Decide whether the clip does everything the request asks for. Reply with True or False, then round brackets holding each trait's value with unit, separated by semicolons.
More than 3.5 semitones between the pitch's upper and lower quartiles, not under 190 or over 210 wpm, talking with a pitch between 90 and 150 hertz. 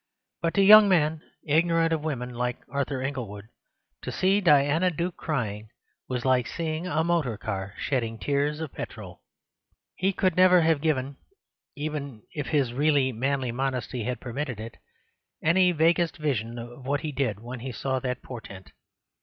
False (4.5 semitones; 160 wpm; 140 Hz)